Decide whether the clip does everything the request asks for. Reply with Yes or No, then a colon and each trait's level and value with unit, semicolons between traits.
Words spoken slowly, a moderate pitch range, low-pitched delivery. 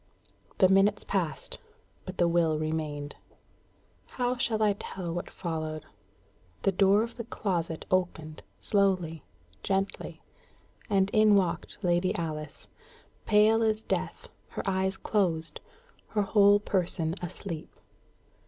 No: slow, 115 wpm; average, 3.8 semitones; high, 190 Hz